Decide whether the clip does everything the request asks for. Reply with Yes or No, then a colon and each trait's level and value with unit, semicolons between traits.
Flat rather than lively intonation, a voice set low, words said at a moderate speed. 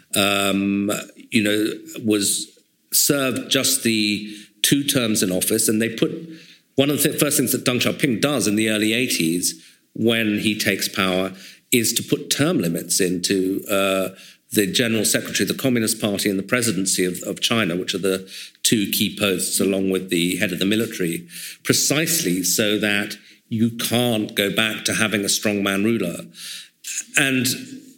No: average, 3.2 semitones; low, 105 Hz; average, 165 wpm